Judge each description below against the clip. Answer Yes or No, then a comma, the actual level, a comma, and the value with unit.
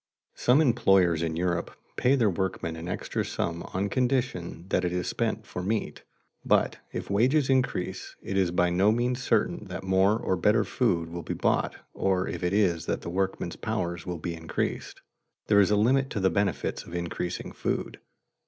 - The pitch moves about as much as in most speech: Yes, average, 4.1 semitones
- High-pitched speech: No, very low, 95 Hz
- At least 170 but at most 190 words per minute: Yes, average, 185 wpm